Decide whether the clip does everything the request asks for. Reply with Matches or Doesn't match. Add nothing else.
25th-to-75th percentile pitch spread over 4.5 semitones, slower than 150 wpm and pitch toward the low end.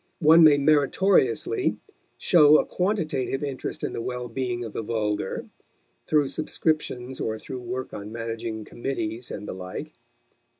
Matches